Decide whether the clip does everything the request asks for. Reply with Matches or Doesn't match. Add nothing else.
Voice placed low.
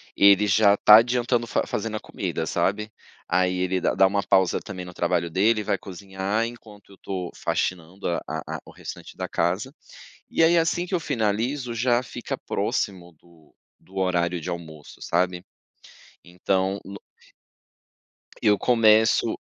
Matches